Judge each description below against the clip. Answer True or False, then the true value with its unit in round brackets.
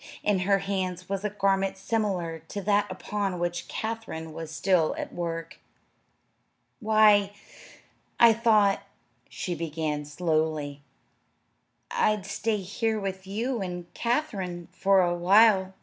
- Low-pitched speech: False (190 Hz)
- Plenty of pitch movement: False (3.1 semitones)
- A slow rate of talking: True (120 wpm)